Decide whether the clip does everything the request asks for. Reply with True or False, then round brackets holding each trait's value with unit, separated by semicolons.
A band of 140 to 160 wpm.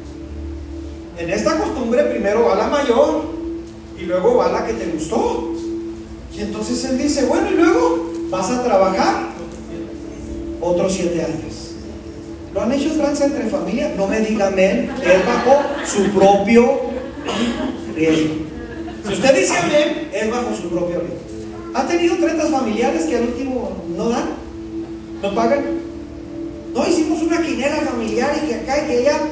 True (150 wpm)